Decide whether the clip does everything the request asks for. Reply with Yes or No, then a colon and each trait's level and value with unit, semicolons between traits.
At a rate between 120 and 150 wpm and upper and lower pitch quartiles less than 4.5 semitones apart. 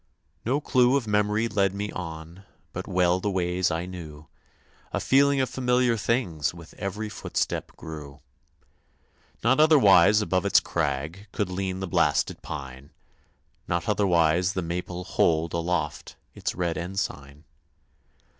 Yes: slow, 135 wpm; average, 4.1 semitones